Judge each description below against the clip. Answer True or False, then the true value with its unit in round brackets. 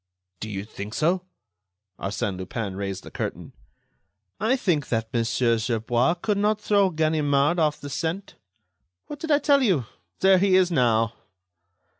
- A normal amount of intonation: False (8.9 semitones)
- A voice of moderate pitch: True (150 Hz)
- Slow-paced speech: False (150 wpm)